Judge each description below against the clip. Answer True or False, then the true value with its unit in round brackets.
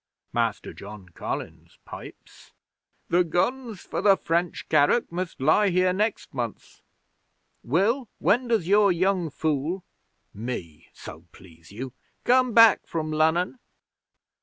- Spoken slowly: True (120 wpm)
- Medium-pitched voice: True (175 Hz)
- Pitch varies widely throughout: True (7.3 semitones)